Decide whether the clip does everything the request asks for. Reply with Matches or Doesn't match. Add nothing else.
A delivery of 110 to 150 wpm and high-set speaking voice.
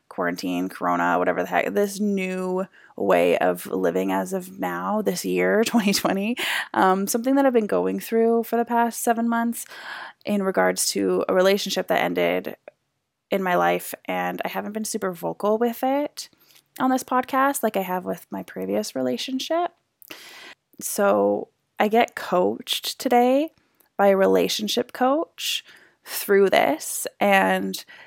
Matches